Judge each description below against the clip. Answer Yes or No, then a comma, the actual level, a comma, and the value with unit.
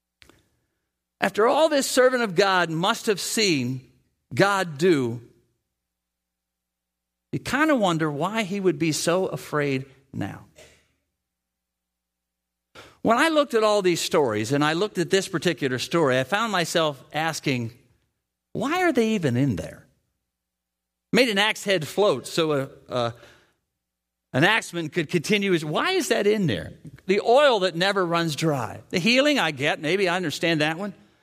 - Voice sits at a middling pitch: Yes, medium, 155 Hz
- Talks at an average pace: Yes, average, 150 wpm